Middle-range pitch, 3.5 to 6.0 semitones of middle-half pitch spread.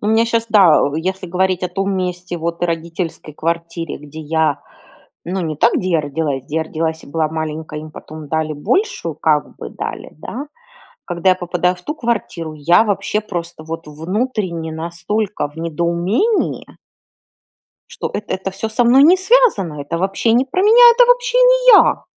Yes: medium, 175 Hz; average, 5.1 semitones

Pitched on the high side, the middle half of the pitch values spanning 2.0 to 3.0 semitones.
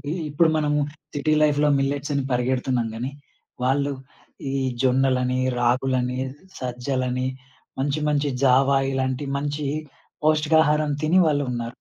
No: low, 135 Hz; narrow, 2.6 semitones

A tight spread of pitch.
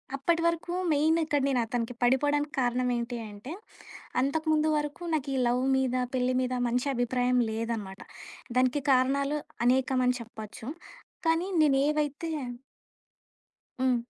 No: average, 3.2 semitones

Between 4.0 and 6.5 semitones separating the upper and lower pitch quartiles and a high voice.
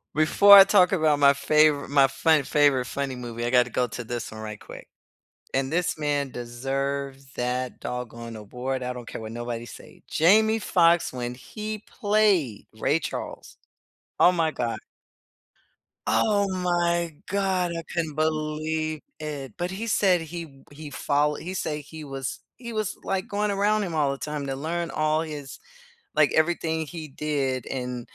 No: average, 4.7 semitones; medium, 150 Hz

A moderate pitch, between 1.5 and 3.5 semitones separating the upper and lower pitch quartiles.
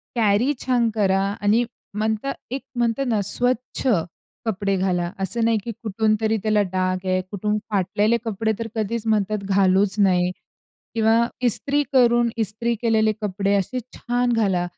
No: high, 215 Hz; average, 3.0 semitones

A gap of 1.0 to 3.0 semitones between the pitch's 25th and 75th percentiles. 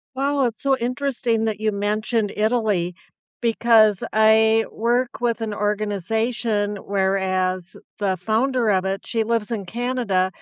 Yes: average, 2.7 semitones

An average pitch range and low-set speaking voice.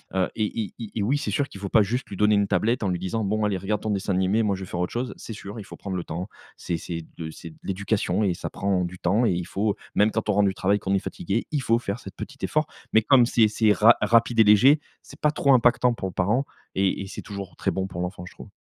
Yes: average, 3.1 semitones; low, 100 Hz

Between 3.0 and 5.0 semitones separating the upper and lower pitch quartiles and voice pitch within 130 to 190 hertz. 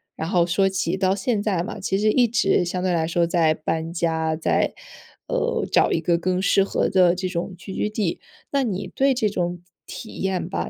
No: narrow, 2.6 semitones; medium, 185 Hz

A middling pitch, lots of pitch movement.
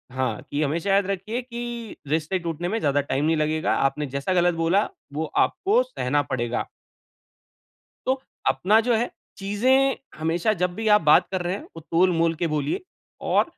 Yes: medium, 175 Hz; wide, 5.8 semitones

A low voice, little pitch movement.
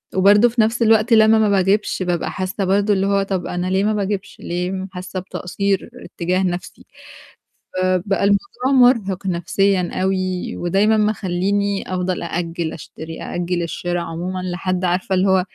No: high, 190 Hz; narrow, 2.0 semitones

